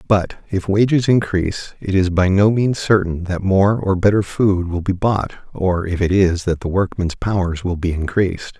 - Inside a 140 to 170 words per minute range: No, average, 200 wpm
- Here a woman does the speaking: No, male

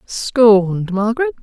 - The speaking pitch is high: Yes, high, 225 Hz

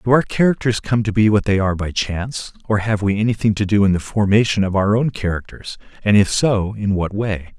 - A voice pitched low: Yes, low, 105 Hz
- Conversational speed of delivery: No, fast, 235 wpm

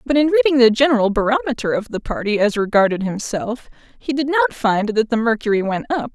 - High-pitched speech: Yes, high, 240 Hz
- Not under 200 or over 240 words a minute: Yes, fast, 205 wpm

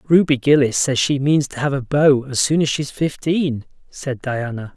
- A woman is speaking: No, male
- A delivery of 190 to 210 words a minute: Yes, average, 200 wpm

